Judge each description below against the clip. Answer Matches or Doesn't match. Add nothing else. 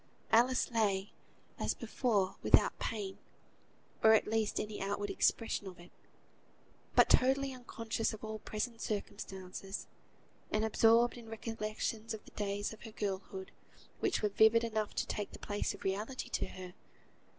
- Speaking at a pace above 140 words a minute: Matches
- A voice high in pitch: Matches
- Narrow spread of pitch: Matches